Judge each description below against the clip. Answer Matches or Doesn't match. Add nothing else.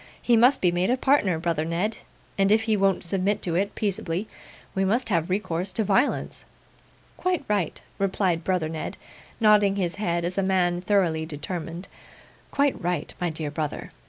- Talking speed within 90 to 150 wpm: Doesn't match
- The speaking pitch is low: Doesn't match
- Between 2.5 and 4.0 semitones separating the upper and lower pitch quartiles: Matches